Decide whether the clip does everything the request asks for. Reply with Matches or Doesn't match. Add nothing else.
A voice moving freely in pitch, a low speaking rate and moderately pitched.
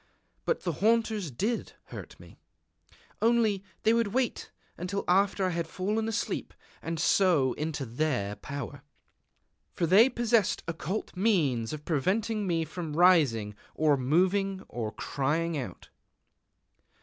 Matches